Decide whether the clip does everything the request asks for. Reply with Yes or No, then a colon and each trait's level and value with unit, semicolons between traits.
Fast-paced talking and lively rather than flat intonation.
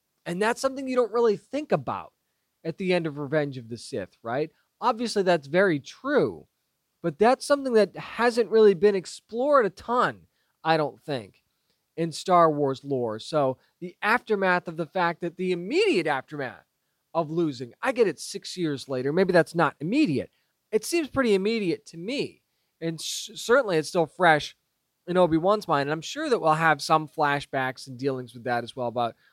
No: average, 185 wpm; wide, 6.7 semitones